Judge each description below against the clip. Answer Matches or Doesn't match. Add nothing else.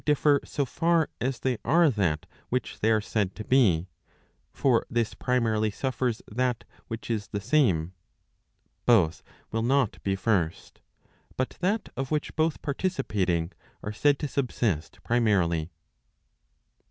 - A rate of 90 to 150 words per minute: Matches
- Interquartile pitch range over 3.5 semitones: Matches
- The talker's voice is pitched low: Matches